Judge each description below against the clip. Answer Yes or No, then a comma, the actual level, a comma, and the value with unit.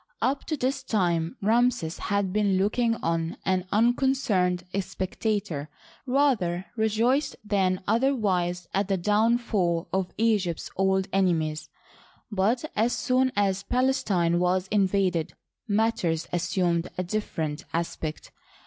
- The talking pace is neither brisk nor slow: No, slow, 120 wpm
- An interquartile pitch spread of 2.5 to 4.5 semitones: Yes, average, 4.1 semitones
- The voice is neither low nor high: No, high, 195 Hz